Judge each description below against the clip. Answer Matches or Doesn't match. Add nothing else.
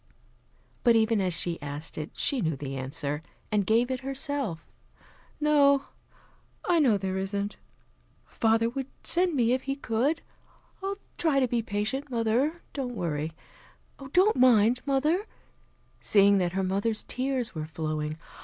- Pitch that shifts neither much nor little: Doesn't match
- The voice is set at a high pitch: Matches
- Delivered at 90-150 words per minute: Matches